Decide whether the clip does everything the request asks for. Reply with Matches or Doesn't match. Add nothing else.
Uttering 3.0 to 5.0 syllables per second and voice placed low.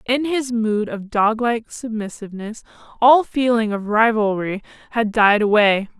Doesn't match